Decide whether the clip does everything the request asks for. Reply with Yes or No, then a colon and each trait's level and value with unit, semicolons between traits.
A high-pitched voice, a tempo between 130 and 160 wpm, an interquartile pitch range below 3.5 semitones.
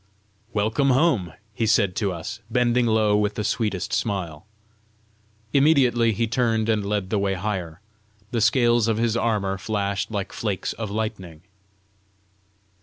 No: low, 110 Hz; average, 140 wpm; average, 2.8 semitones